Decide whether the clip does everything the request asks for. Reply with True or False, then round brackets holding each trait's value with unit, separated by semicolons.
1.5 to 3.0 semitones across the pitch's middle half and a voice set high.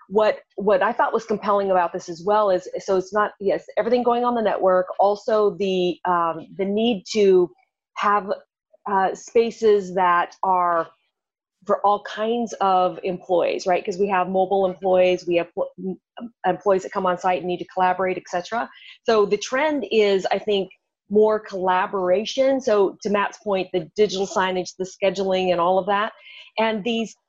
True (2.6 semitones; 195 Hz)